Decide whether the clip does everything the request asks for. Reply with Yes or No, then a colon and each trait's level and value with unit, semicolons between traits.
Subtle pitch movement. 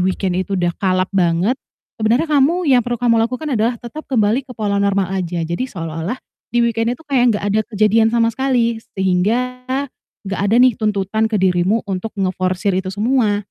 No: average, 4.2 semitones